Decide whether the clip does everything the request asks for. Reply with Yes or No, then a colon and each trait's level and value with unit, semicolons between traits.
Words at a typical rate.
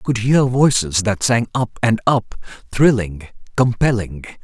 Yes: average, 150 wpm